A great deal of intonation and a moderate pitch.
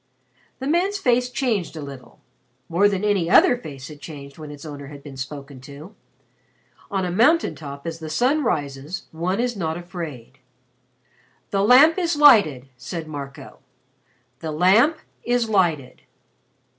Yes: wide, 8.6 semitones; medium, 170 Hz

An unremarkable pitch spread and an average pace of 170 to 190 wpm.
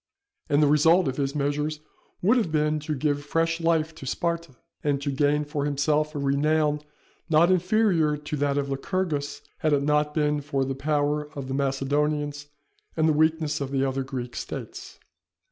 No: narrow, 1.8 semitones; average, 180 wpm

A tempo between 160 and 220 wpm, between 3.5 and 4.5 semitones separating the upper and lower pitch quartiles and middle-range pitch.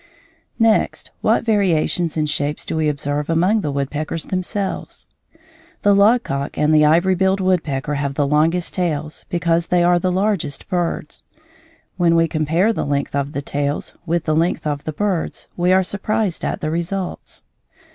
Yes: average, 165 wpm; average, 3.8 semitones; medium, 165 Hz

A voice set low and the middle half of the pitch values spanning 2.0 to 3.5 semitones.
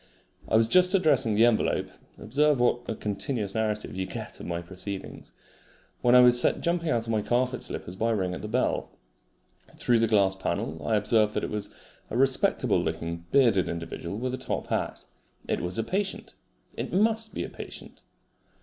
No: low, 115 Hz; average, 4.5 semitones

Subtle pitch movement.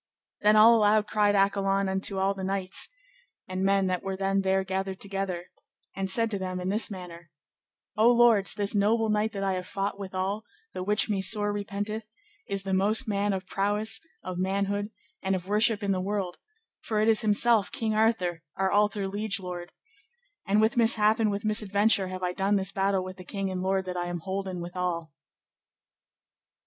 Yes: narrow, 1.9 semitones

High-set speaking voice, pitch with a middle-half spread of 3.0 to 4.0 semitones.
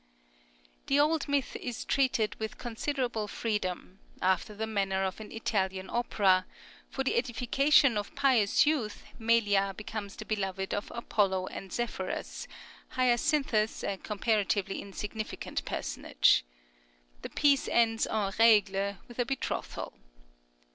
Yes: high, 215 Hz; average, 3.6 semitones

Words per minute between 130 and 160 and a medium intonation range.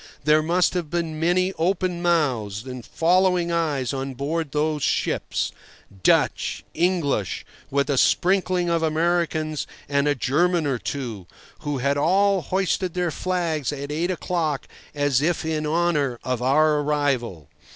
Yes: slow, 135 wpm; average, 3.7 semitones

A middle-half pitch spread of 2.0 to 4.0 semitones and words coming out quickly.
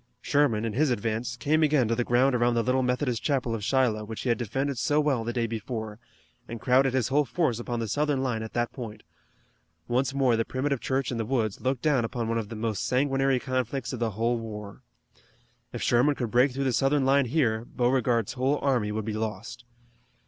Yes: average, 2.9 semitones; fast, 215 wpm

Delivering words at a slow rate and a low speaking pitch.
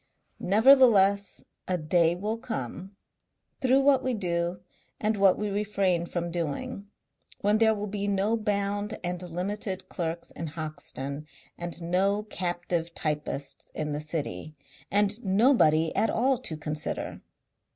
No: slow, 130 wpm; high, 190 Hz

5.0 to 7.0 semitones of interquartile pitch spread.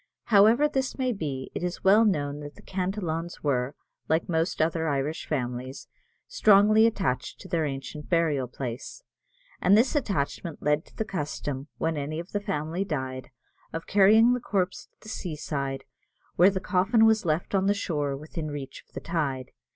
Yes: wide, 5.6 semitones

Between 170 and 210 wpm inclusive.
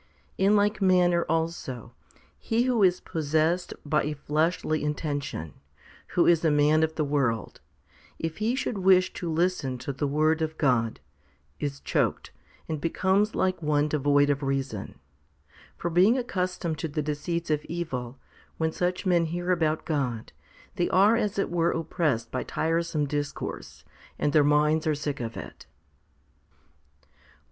No: average, 155 wpm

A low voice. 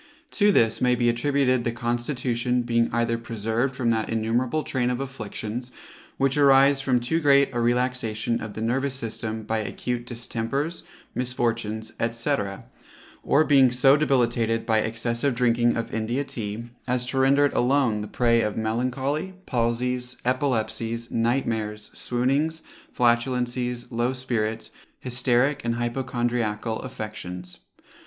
Yes: low, 120 Hz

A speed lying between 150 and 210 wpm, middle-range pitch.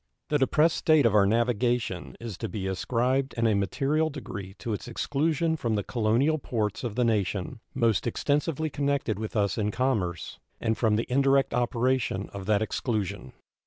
No: average, 170 wpm; low, 115 Hz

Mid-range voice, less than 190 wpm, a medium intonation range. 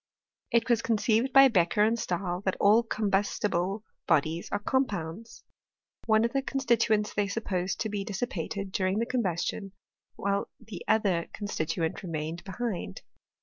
No: high, 205 Hz; average, 145 wpm; average, 4.1 semitones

